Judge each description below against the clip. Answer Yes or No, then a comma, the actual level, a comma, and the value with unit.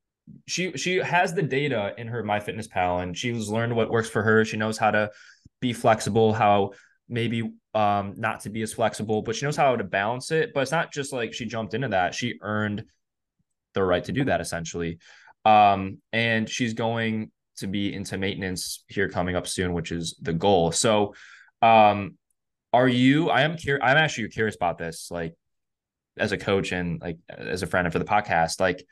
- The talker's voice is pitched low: Yes, low, 110 Hz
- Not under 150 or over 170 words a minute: No, average, 200 wpm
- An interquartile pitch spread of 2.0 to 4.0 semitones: Yes, average, 3.2 semitones